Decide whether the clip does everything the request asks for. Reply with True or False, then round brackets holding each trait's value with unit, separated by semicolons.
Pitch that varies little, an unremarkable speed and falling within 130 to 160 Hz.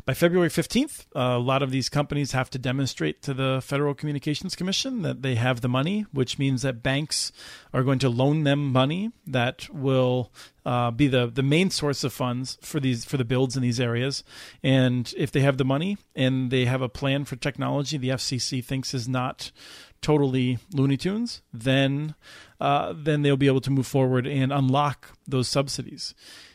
True (2.0 semitones; 190 wpm; 135 Hz)